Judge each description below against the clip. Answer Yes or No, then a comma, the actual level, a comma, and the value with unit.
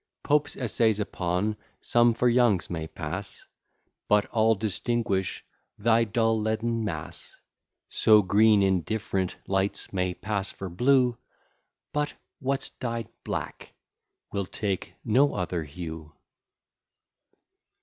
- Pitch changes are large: No, average, 3.8 semitones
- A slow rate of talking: Yes, slow, 110 wpm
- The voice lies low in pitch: Yes, low, 105 Hz